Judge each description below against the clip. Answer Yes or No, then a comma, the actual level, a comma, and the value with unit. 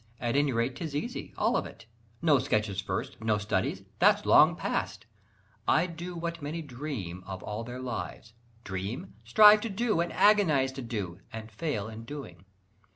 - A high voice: No, low, 125 Hz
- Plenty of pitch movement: Yes, wide, 7.0 semitones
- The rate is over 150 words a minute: Yes, average, 170 wpm